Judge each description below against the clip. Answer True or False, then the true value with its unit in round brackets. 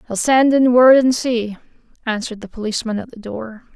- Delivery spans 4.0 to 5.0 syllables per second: False (5.6 syllables/s)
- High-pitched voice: True (235 Hz)